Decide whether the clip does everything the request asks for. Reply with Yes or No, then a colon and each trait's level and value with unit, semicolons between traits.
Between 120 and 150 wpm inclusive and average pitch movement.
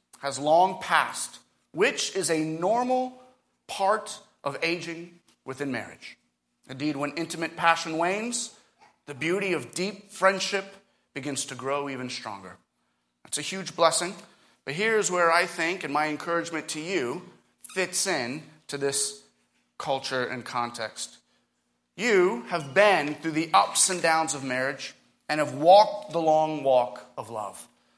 No: average, 140 wpm; wide, 5.7 semitones